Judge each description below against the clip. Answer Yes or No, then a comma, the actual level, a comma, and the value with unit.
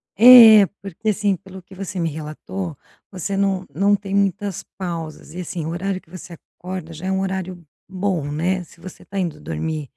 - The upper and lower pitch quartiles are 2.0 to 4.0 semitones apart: Yes, average, 2.8 semitones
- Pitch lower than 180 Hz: No, medium, 185 Hz